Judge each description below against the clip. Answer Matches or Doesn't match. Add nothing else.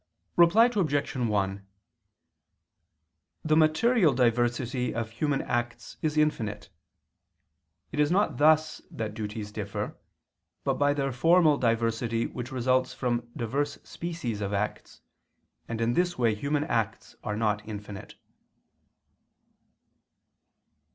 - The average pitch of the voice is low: Matches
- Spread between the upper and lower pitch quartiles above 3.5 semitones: Matches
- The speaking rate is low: Matches